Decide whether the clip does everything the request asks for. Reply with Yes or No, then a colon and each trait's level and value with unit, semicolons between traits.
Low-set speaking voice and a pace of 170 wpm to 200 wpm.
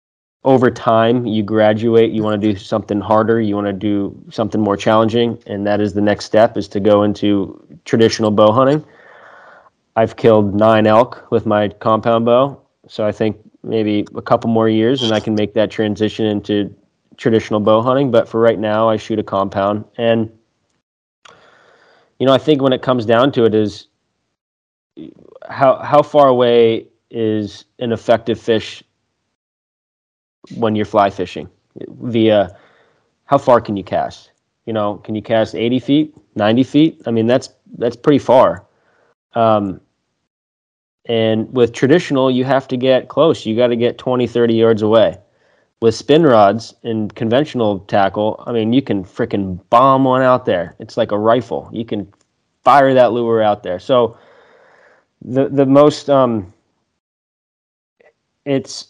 No: low, 110 Hz; average, 160 wpm